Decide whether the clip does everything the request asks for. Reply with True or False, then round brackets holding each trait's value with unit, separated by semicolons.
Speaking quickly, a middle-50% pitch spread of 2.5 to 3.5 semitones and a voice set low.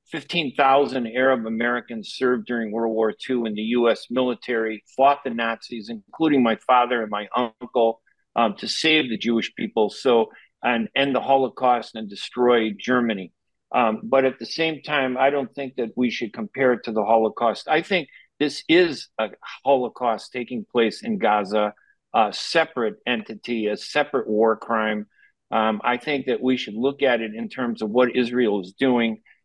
True (175 wpm; 3.1 semitones; 120 Hz)